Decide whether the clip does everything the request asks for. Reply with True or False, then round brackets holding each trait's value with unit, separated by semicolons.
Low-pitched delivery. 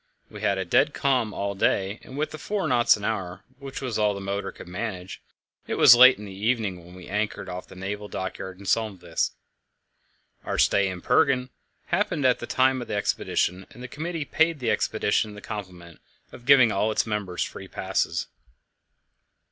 True (105 Hz)